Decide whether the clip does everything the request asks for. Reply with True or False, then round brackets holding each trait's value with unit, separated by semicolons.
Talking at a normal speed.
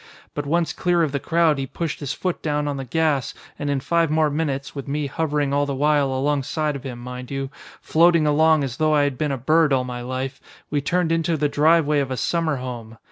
False (235 wpm)